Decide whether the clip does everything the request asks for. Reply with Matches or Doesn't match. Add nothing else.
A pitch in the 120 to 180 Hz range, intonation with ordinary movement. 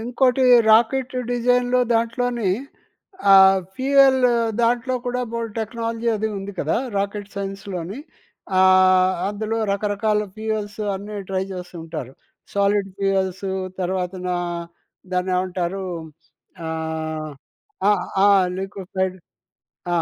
Doesn't match